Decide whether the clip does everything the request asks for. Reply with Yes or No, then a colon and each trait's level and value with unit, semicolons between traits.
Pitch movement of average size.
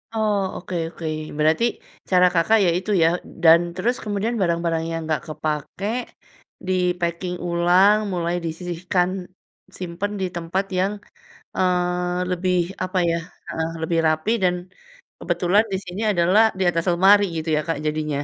No: narrow, 2.0 semitones